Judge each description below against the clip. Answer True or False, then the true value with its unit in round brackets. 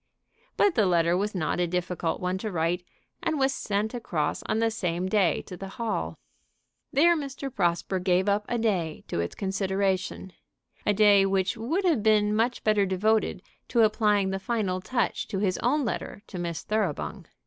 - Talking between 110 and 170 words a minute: False (180 wpm)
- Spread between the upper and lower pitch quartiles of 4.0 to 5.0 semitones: False (3.6 semitones)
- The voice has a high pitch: True (200 Hz)